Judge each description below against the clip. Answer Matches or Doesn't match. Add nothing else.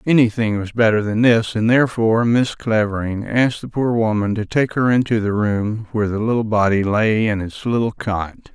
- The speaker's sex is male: Matches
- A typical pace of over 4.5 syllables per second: Matches